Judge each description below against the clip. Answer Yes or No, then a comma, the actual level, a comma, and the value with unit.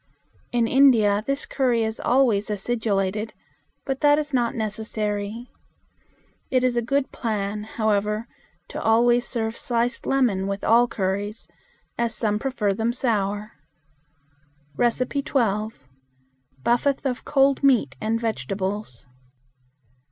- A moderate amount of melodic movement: Yes, average, 3.2 semitones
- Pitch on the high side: Yes, high, 225 Hz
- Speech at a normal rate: No, slow, 115 wpm